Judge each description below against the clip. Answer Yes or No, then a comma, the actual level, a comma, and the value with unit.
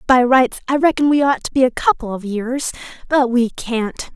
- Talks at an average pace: No, fast, 215 wpm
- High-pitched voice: Yes, very high, 250 Hz